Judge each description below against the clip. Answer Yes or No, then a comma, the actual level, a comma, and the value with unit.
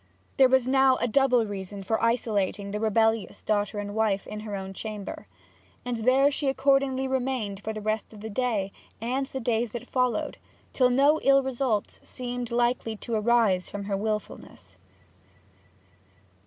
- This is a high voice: Yes, high, 225 Hz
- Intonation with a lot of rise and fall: No, average, 3.7 semitones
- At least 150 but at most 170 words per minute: Yes, average, 160 wpm